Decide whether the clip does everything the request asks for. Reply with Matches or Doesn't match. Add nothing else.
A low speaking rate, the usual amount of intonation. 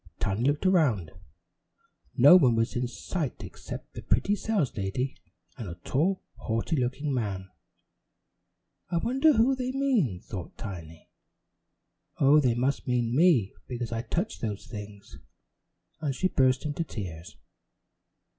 Doesn't match